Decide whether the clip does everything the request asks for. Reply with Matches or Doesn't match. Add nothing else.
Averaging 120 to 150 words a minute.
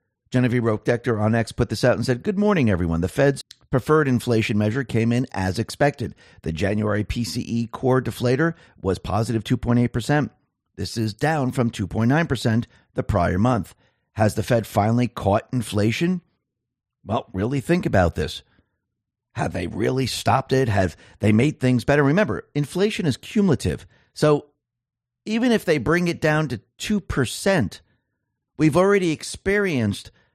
Matches